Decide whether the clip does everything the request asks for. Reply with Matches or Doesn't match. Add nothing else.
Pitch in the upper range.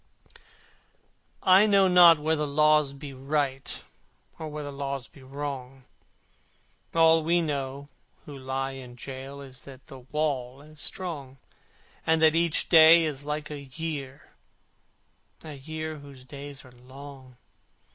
Doesn't match